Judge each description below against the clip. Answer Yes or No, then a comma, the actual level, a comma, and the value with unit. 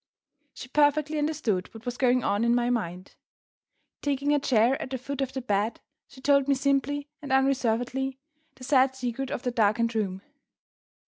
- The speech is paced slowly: No, average, 175 wpm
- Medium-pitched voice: No, very high, 260 Hz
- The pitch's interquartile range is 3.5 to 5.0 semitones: No, average, 3.0 semitones